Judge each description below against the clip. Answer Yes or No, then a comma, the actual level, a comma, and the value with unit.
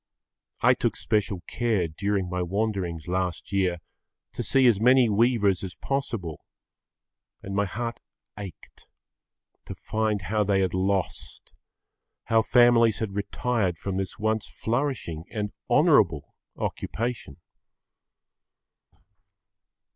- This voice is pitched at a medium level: No, low, 100 Hz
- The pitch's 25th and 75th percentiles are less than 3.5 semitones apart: No, average, 3.9 semitones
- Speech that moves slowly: Yes, slow, 110 wpm